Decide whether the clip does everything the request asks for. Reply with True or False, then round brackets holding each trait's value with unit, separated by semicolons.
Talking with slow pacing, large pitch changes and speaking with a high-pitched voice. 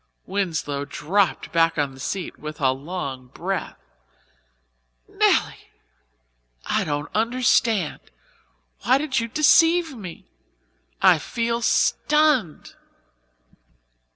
True (95 wpm; 8.2 semitones; 195 Hz)